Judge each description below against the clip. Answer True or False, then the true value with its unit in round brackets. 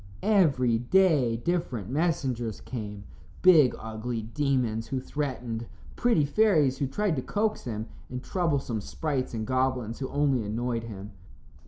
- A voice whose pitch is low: True (130 Hz)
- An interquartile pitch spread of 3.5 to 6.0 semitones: True (4.8 semitones)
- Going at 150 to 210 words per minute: False (135 wpm)